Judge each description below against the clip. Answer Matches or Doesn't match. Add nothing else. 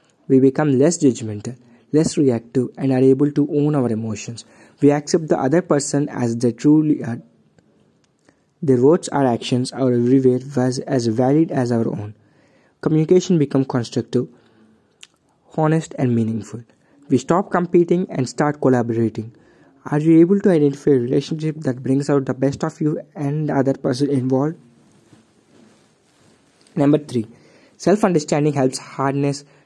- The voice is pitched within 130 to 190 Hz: Matches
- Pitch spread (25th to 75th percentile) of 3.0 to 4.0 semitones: Matches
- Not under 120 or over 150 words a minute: Matches